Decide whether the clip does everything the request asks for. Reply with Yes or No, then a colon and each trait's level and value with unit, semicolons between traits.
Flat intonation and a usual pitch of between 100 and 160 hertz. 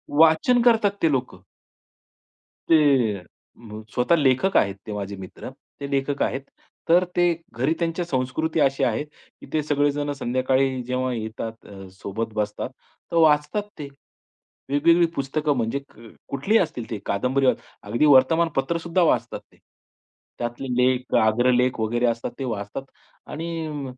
No: average, 4.6 semitones; low, 135 Hz